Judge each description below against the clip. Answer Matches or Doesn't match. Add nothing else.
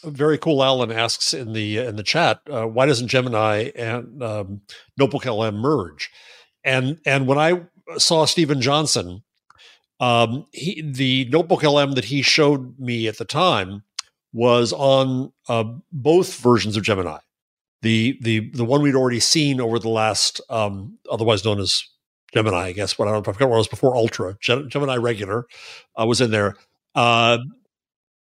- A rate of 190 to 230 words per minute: Doesn't match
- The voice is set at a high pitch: Doesn't match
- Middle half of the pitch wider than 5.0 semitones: Doesn't match